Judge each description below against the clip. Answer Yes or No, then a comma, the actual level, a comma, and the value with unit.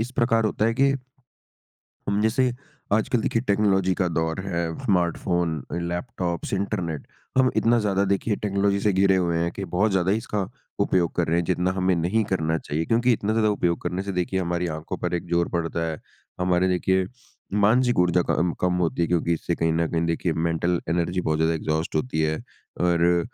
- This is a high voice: No, very low, 90 Hz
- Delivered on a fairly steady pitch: No, average, 3.1 semitones